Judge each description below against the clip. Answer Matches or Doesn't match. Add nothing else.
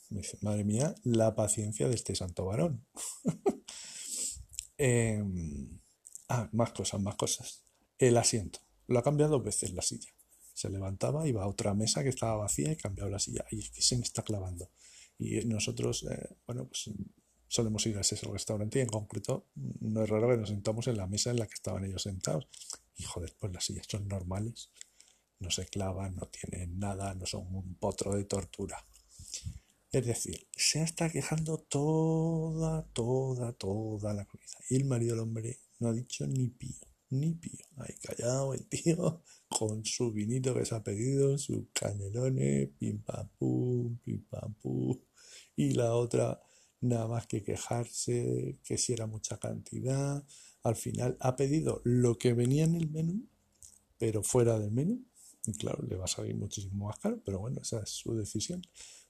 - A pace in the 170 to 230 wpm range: Matches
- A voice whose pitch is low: Matches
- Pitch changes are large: Doesn't match